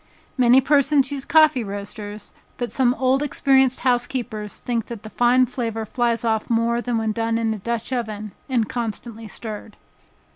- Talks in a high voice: Yes, high, 235 Hz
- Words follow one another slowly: No, average, 160 wpm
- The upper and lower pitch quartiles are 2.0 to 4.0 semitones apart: Yes, narrow, 2.6 semitones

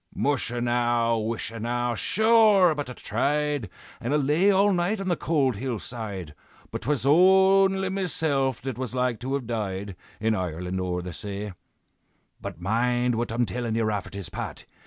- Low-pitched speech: Yes, low, 120 Hz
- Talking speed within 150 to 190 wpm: Yes, average, 165 wpm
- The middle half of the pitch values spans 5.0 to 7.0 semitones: Yes, wide, 5.5 semitones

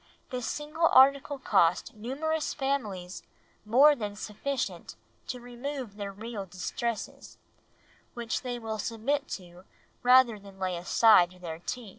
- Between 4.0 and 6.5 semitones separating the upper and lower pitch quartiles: Yes, average, 5.2 semitones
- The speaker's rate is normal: No, slow, 125 wpm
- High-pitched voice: Yes, high, 230 Hz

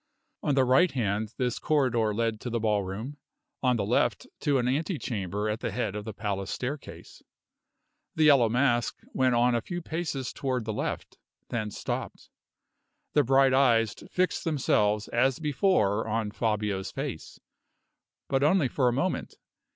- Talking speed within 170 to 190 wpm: No, average, 160 wpm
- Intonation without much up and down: No, average, 4.2 semitones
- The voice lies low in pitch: Yes, low, 120 Hz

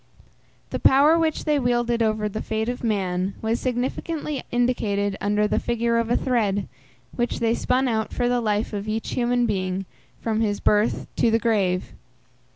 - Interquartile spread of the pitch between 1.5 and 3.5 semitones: Yes, average, 2.8 semitones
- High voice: Yes, high, 225 Hz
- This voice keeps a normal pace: Yes, average, 170 wpm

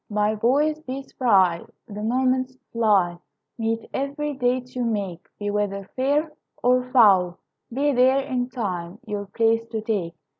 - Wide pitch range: No, average, 4.1 semitones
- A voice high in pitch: Yes, high, 230 Hz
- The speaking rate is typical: Yes, average, 145 wpm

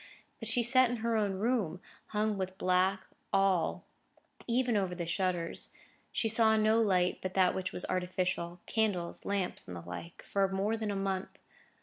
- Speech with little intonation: No, average, 3.2 semitones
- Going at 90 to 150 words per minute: No, average, 160 wpm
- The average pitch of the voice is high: Yes, high, 195 Hz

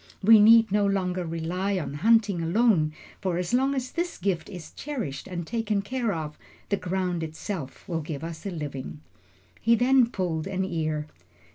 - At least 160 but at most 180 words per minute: Yes, average, 170 wpm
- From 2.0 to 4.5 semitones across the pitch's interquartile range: No, average, 5.3 semitones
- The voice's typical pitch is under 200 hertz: Yes, medium, 185 Hz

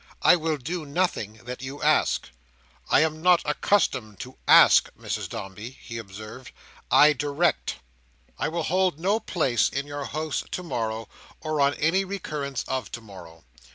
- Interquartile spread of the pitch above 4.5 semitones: Yes, wide, 5.5 semitones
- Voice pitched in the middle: Yes, medium, 145 Hz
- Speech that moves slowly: No, average, 155 wpm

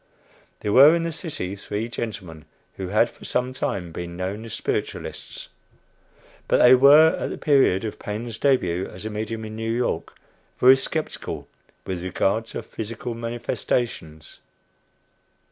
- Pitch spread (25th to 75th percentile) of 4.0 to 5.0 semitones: Yes, average, 4.7 semitones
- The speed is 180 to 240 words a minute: No, average, 145 wpm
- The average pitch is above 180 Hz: No, low, 110 Hz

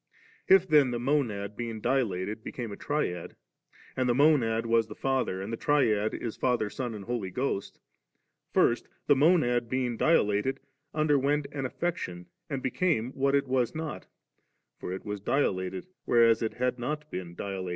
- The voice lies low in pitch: Yes, low, 120 Hz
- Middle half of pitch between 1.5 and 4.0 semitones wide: No, average, 4.8 semitones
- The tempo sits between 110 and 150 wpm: No, average, 165 wpm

